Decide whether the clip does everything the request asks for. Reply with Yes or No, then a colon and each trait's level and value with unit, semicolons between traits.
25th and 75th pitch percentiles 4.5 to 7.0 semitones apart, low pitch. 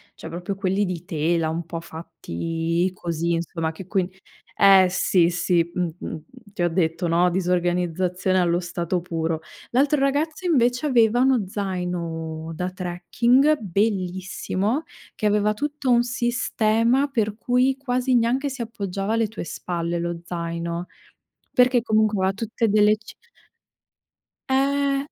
No: wide, 5.6 semitones; high, 190 Hz